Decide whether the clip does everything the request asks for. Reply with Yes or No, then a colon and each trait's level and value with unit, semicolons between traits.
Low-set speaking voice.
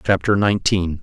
Yes: very low, 95 Hz